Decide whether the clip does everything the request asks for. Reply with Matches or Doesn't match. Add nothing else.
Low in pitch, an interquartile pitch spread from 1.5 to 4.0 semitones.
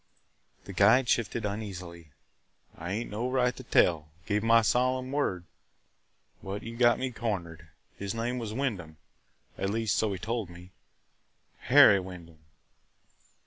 Doesn't match